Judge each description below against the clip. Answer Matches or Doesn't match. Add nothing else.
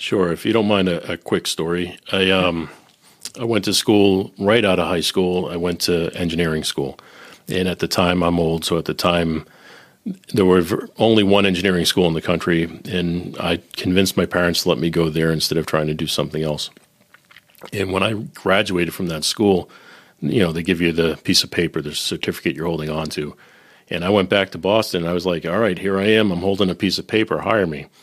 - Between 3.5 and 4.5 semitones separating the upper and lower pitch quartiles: Doesn't match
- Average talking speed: Doesn't match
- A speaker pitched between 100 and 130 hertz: Doesn't match